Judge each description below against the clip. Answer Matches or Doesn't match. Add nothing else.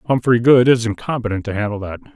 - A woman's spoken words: Doesn't match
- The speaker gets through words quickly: Doesn't match